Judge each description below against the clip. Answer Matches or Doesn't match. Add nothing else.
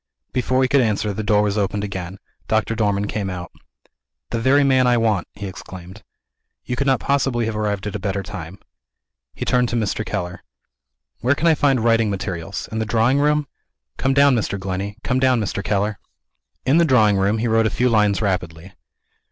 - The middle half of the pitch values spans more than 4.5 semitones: Doesn't match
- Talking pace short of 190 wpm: Doesn't match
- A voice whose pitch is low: Matches